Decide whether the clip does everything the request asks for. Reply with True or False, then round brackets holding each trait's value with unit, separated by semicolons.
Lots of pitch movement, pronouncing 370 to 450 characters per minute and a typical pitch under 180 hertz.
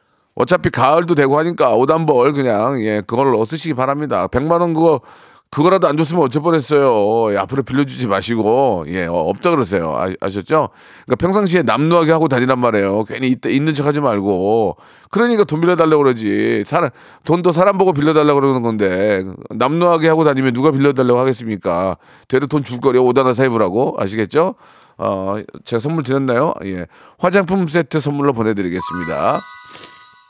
False (4.8 semitones; 380 characters per minute; 135 Hz)